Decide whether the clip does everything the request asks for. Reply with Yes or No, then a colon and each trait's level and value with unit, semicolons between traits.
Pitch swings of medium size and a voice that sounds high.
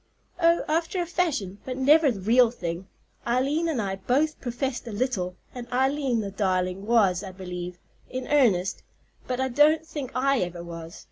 No: wide, 6.6 semitones; high, 245 Hz